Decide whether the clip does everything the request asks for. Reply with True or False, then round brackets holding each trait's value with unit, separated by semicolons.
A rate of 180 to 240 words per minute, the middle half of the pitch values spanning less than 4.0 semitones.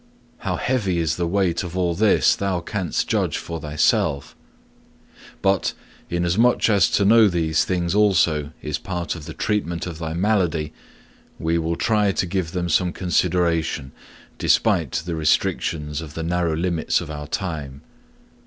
False (155 wpm; 3.0 semitones)